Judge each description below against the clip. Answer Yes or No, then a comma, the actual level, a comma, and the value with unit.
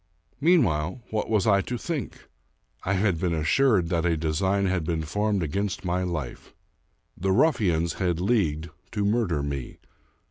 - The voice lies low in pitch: Yes, very low, 95 Hz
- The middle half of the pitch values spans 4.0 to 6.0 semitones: Yes, average, 4.4 semitones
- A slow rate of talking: No, average, 150 wpm